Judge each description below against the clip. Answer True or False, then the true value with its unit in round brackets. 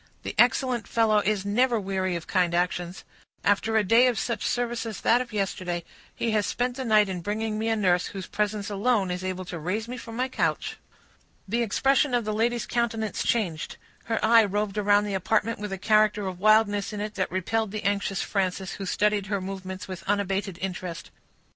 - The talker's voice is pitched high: True (210 Hz)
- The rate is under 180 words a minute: False (200 wpm)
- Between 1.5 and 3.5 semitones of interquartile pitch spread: True (2.9 semitones)